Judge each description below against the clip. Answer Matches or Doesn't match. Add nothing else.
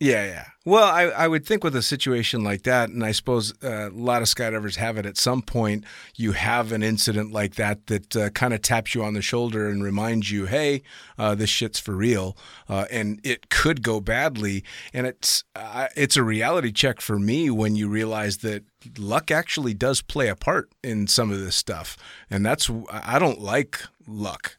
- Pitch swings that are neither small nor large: Matches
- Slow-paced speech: Doesn't match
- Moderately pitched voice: Doesn't match